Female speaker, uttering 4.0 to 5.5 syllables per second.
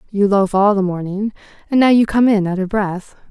Yes: female; 5.3 syllables/s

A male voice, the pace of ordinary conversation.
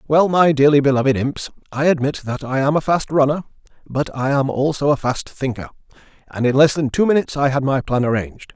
No: male; fast, 215 wpm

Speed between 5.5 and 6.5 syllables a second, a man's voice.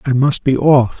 No: 4.5 syllables/s; male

